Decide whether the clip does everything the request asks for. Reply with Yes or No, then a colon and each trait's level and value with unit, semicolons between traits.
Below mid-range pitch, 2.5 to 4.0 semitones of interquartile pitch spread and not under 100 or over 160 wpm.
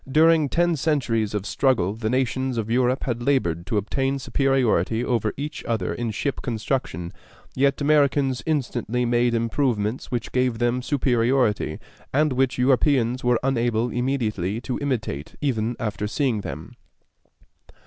Yes: low, 125 Hz; average, 3.2 semitones; average, 140 wpm